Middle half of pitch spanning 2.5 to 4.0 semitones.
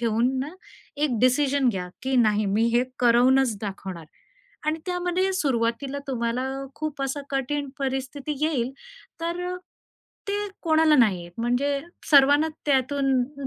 Yes: average, 3.6 semitones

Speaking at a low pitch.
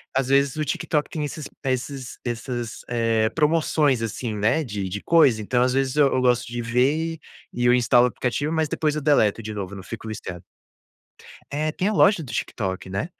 Yes: low, 125 Hz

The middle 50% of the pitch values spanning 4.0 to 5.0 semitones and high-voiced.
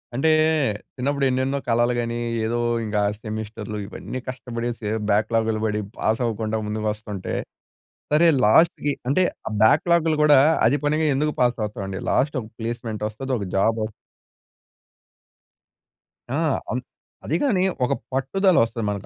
No: average, 4.4 semitones; low, 120 Hz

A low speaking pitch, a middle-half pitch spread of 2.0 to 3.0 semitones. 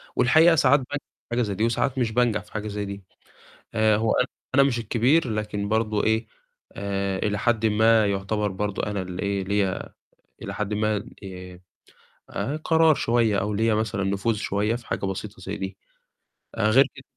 Yes: low, 105 Hz; narrow, 2.5 semitones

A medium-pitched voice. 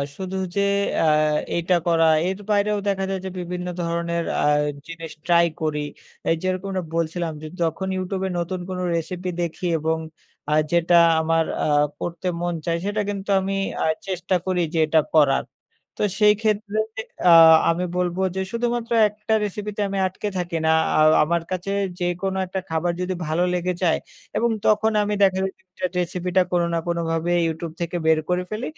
Yes: medium, 180 Hz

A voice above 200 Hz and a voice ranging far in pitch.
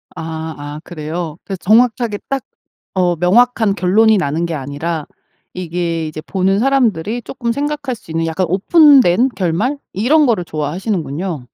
No: medium, 185 Hz; wide, 6.4 semitones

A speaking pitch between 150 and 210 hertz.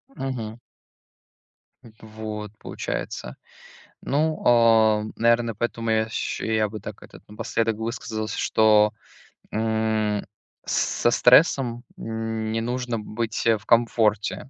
No: low, 110 Hz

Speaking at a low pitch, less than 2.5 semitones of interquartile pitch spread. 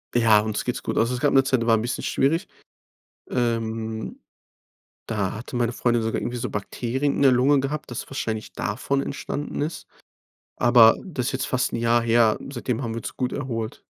No: low, 120 Hz; average, 2.8 semitones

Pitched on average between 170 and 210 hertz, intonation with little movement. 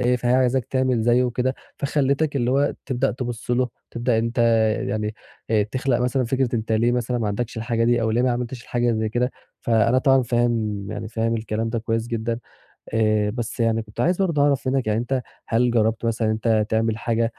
No: low, 120 Hz; narrow, 2.1 semitones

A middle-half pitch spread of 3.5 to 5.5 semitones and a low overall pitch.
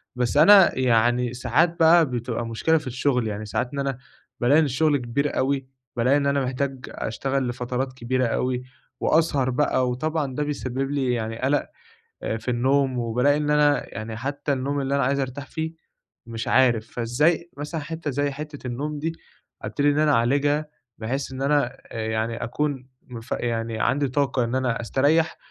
No: average, 3.1 semitones; low, 130 Hz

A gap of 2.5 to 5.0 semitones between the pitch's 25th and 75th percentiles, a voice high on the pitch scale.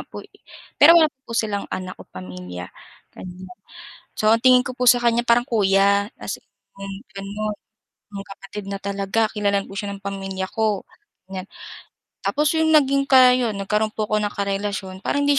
Yes: average, 3.4 semitones; high, 205 Hz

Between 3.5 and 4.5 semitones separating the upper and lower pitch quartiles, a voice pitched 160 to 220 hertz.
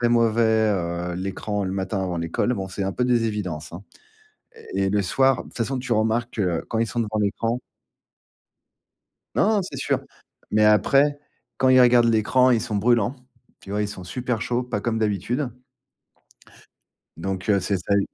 No: average, 3.8 semitones; low, 110 Hz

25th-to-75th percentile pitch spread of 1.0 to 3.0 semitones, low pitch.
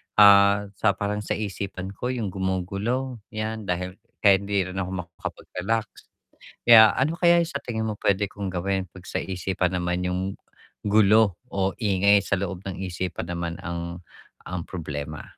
Yes: narrow, 2.6 semitones; very low, 95 Hz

